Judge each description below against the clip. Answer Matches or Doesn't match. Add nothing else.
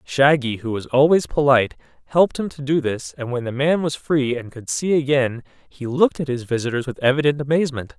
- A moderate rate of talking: Doesn't match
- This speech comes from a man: Matches